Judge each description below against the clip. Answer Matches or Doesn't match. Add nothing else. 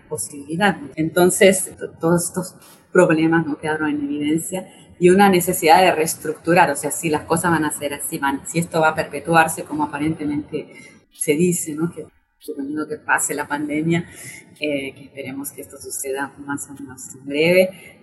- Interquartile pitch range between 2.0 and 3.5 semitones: Matches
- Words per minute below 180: Matches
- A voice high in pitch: Doesn't match